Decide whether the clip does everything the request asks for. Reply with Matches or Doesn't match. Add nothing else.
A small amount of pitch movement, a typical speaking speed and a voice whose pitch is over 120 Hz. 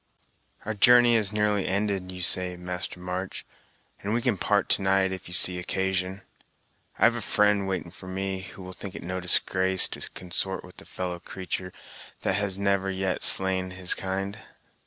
Doesn't match